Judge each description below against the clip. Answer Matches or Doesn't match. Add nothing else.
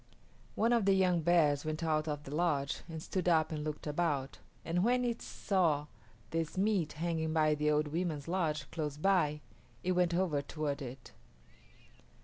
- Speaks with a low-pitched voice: Doesn't match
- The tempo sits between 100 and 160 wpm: Doesn't match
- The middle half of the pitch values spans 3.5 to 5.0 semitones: Doesn't match